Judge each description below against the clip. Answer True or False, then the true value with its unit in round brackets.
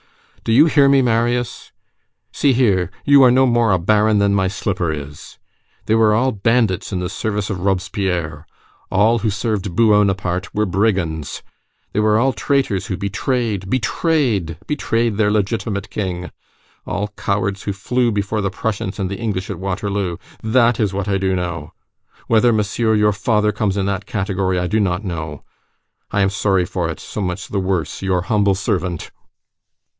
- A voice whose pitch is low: True (100 Hz)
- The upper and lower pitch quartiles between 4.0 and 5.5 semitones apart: False (3.0 semitones)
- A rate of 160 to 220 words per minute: True (175 wpm)